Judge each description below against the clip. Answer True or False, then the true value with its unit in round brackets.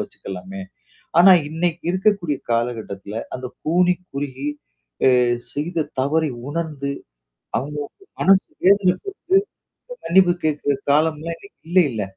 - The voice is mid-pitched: True (155 Hz)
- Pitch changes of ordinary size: True (4.6 semitones)